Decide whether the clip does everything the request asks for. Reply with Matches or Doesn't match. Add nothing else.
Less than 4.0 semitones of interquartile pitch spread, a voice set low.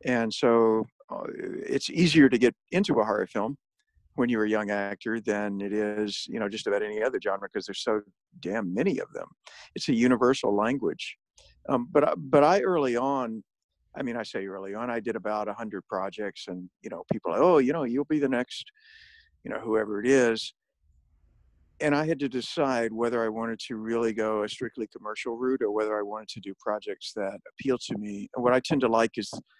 Matches